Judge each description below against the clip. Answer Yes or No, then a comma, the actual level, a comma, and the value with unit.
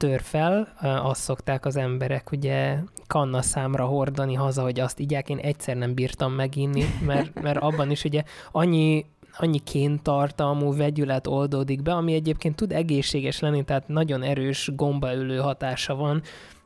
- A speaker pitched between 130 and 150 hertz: Yes, medium, 140 Hz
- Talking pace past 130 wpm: Yes, average, 150 wpm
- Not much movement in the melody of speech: Yes, narrow, 1.8 semitones